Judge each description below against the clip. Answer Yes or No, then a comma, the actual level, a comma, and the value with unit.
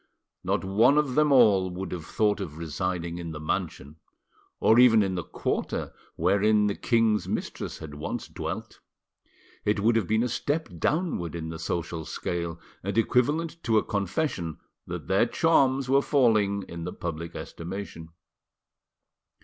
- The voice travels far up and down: Yes, wide, 6.0 semitones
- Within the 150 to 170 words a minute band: Yes, average, 155 wpm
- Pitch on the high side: No, low, 100 Hz